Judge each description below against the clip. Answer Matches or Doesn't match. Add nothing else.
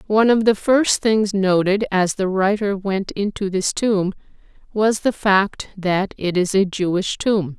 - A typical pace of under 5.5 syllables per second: Matches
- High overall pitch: Matches